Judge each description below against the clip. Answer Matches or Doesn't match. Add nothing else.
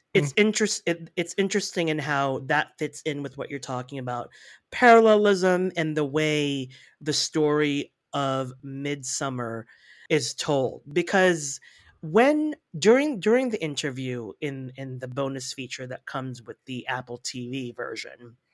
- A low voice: Doesn't match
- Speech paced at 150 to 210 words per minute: Doesn't match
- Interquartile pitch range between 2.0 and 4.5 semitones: Doesn't match